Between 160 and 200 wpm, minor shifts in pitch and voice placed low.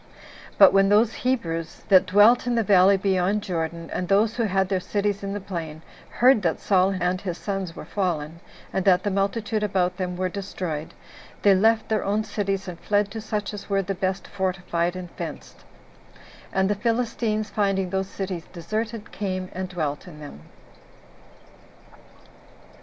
No: average, 170 wpm; narrow, 2.3 semitones; high, 195 Hz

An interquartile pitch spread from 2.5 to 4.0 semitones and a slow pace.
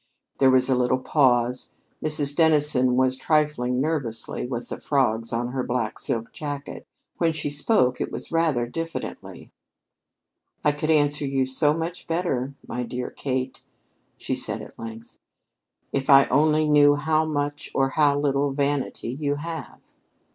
No: average, 3.0 semitones; average, 150 wpm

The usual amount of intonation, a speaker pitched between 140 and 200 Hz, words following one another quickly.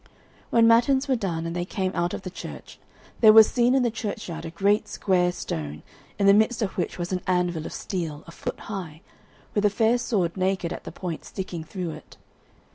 Yes: average, 3.9 semitones; high, 190 Hz; fast, 210 wpm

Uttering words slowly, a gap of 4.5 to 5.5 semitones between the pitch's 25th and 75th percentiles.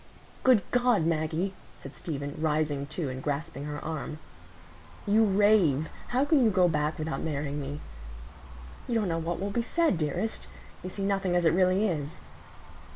No: average, 165 wpm; average, 5.2 semitones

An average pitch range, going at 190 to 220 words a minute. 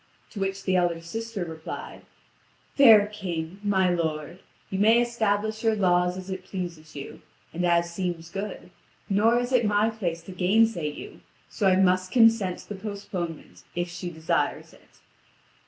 No: average, 3.4 semitones; average, 160 wpm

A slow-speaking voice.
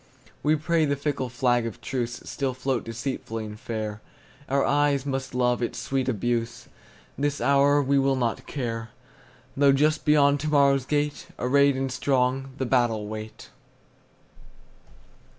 Yes: slow, 125 wpm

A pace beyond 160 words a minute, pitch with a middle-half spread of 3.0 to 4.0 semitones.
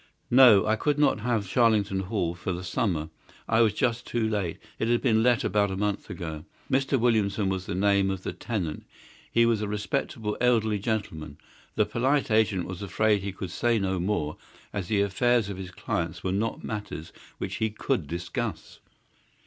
Yes: average, 185 wpm; average, 3.4 semitones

